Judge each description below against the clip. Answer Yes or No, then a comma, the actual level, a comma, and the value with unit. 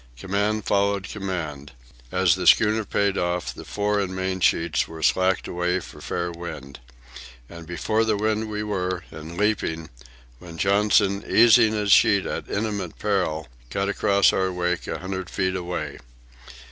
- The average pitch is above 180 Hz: No, very low, 95 Hz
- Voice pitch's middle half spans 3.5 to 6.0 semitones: No, average, 2.8 semitones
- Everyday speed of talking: Yes, average, 155 wpm